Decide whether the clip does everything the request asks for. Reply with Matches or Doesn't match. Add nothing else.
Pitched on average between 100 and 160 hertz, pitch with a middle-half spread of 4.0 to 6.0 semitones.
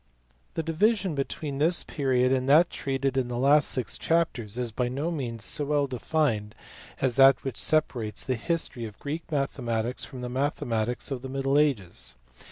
Doesn't match